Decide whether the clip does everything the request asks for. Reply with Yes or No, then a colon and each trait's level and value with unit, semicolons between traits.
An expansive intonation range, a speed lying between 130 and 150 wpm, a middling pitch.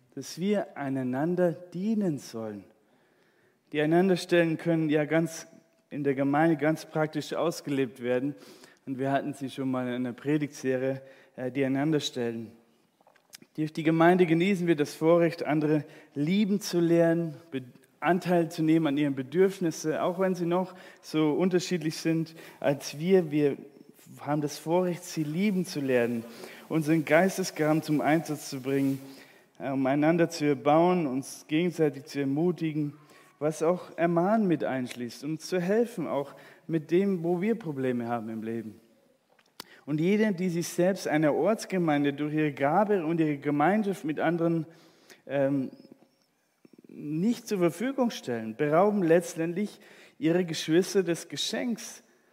No: average, 4.0 semitones; average, 135 wpm; medium, 155 Hz